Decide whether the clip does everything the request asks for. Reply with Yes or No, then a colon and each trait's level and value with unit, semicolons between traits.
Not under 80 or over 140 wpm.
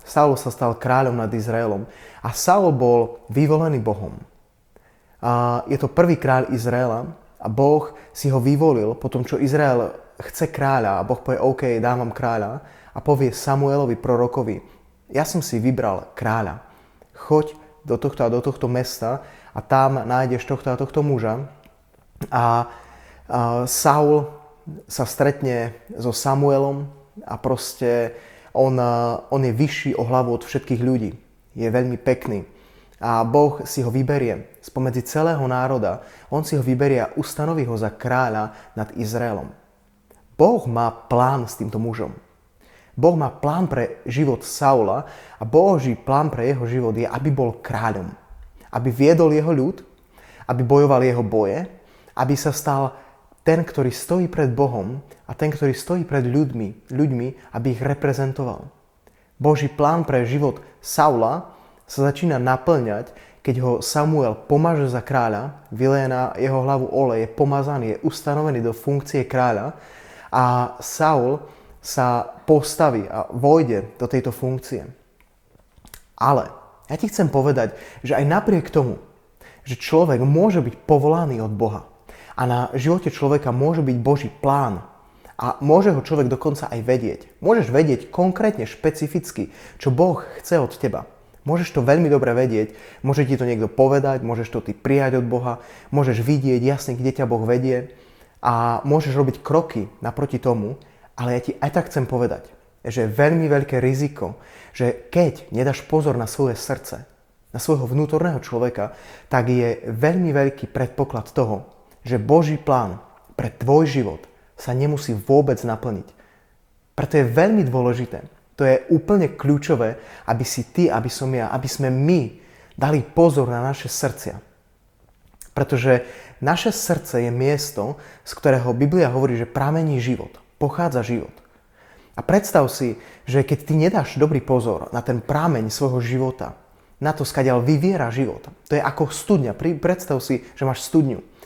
No: average, 150 wpm